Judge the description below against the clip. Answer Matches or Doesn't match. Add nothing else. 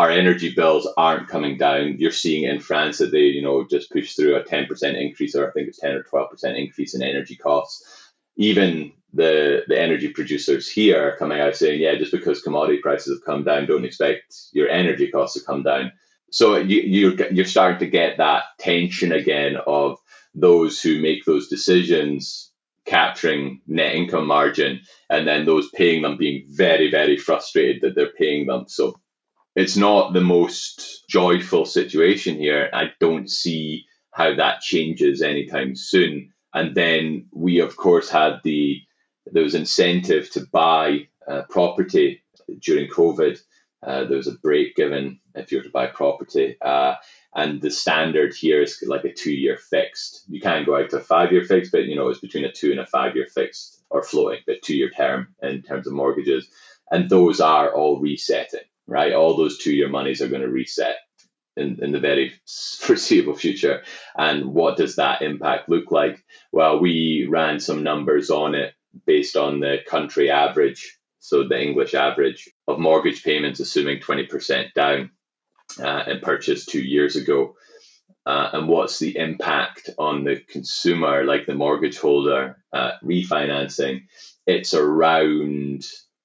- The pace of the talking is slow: Doesn't match